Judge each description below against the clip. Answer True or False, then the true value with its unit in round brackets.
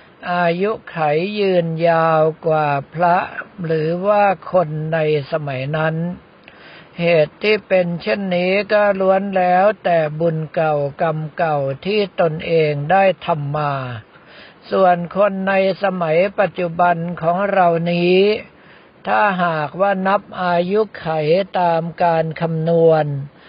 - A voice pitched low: False (170 Hz)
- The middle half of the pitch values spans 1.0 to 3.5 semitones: True (3.2 semitones)